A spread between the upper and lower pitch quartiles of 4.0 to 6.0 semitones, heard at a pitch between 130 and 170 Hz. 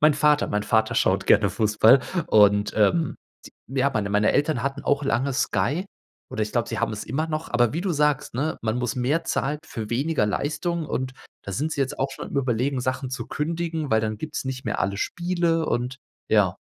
Yes: average, 5.2 semitones; low, 135 Hz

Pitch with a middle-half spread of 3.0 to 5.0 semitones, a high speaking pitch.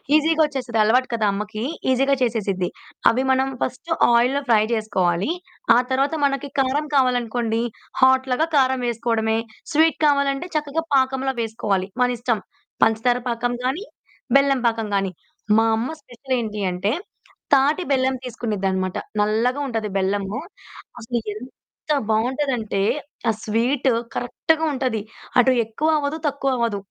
Yes: average, 3.6 semitones; high, 245 Hz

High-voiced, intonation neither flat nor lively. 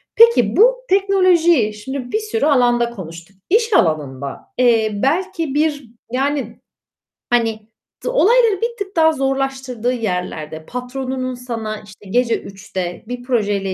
No: very high, 250 Hz; wide, 7.2 semitones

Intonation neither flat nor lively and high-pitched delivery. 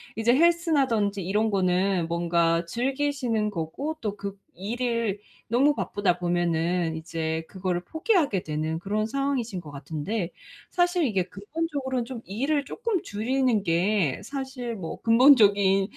No: wide, 6.9 semitones; high, 210 Hz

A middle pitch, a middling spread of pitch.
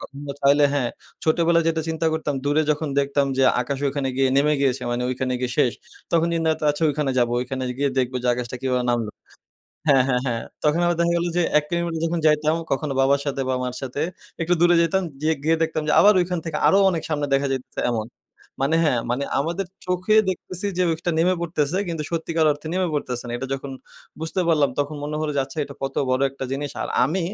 Yes: medium, 150 Hz; average, 3.5 semitones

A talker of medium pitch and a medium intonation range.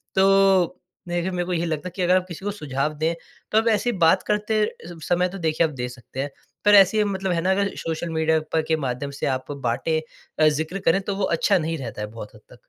Yes: medium, 170 Hz; average, 4.0 semitones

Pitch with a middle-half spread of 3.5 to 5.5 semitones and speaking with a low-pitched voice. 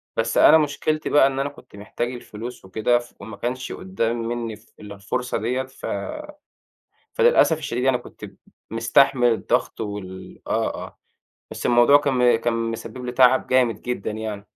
No: average, 2.8 semitones; low, 120 Hz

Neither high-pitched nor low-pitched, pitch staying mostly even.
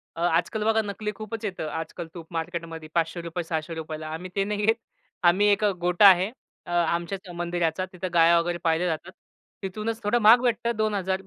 No: medium, 175 Hz; average, 3.7 semitones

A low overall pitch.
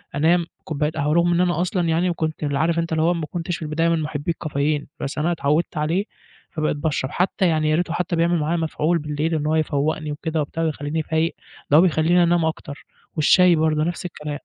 No: medium, 160 Hz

